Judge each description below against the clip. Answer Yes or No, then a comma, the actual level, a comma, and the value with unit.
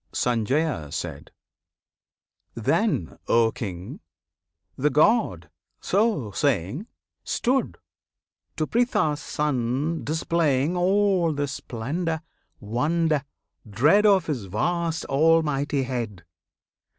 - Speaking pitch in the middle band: Yes, medium, 150 Hz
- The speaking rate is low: Yes, slow, 80 wpm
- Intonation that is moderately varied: No, wide, 6.2 semitones